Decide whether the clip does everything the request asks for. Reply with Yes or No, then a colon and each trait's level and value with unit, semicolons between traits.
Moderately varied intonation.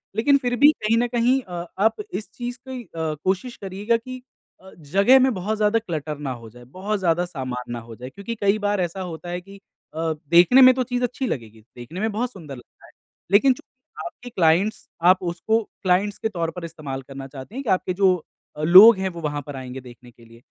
No: wide, 6.9 semitones